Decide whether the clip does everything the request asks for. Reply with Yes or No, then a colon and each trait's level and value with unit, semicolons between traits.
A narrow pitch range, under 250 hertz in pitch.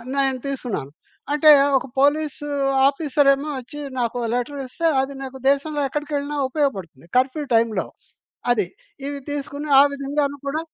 No: narrow, 2.2 semitones; very high, 280 Hz